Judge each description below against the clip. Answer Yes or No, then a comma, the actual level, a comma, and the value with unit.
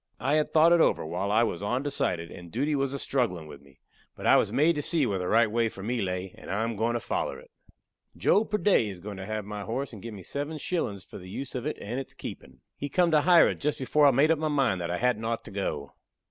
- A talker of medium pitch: No, low, 115 Hz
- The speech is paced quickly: Yes, fast, 275 wpm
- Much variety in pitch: Yes, wide, 6.8 semitones